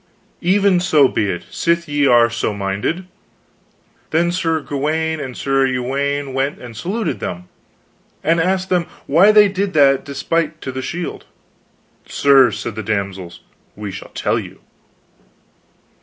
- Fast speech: No, average, 140 wpm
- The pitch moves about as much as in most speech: No, wide, 5.9 semitones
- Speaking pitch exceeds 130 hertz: Yes, medium, 140 Hz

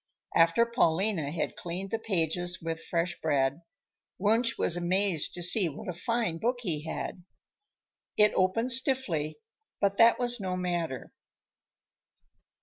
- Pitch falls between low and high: Yes, medium, 180 Hz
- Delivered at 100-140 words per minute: Yes, slow, 135 wpm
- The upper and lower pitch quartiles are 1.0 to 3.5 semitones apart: No, average, 5.2 semitones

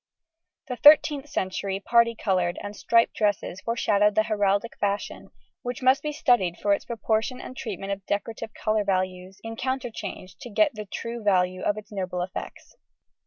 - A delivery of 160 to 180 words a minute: Yes, average, 165 wpm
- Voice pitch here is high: Yes, high, 210 Hz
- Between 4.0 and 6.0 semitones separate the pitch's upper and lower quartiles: No, average, 3.3 semitones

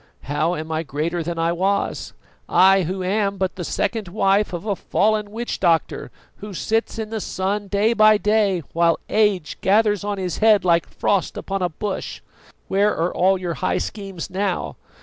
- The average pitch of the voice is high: Yes, high, 195 Hz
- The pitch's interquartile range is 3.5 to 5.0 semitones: No, average, 3.0 semitones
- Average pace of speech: Yes, average, 180 wpm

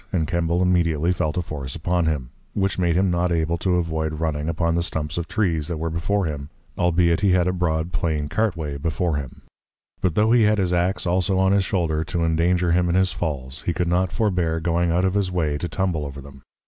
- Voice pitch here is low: Yes, very low, 85 Hz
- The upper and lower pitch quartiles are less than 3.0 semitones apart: Yes, narrow, 2.4 semitones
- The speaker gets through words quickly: Yes, fast, 230 wpm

